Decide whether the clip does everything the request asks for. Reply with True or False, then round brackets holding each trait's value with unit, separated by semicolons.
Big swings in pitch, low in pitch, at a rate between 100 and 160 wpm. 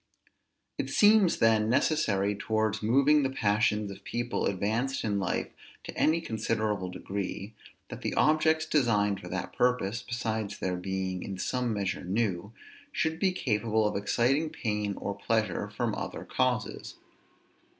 False (4.0 semitones; 110 Hz; 140 wpm)